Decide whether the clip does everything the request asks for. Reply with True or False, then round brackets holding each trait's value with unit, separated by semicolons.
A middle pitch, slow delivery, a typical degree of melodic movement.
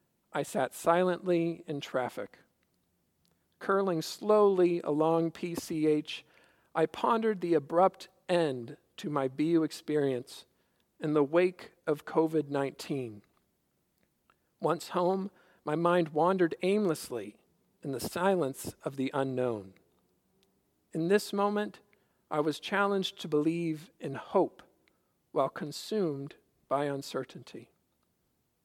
True (165 Hz; 105 wpm; 3.7 semitones)